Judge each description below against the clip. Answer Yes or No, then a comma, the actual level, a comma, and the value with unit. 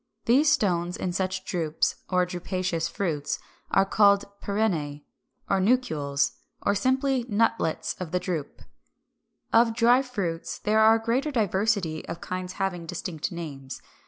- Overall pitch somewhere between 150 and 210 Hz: Yes, high, 190 Hz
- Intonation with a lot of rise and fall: No, average, 4.8 semitones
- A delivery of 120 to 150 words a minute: Yes, average, 140 wpm